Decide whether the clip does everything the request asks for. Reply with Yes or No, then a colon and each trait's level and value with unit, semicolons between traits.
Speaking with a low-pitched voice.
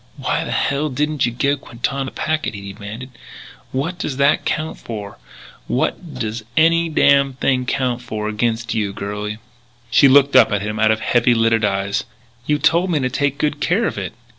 Yes: low, 130 Hz